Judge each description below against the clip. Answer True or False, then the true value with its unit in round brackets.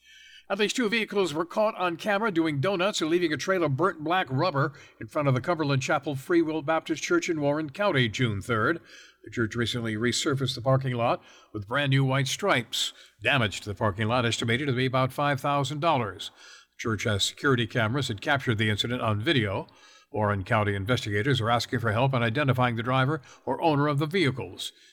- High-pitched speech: False (135 Hz)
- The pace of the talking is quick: False (195 wpm)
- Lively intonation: True (5.7 semitones)